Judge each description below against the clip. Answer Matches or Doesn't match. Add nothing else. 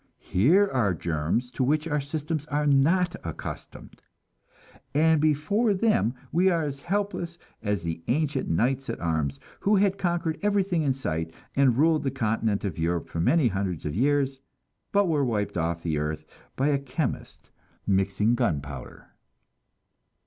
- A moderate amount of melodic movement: Doesn't match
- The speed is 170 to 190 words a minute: Doesn't match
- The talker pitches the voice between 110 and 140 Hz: Matches